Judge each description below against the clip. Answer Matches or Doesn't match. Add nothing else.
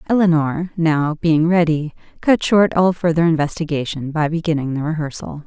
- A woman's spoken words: Matches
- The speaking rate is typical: Matches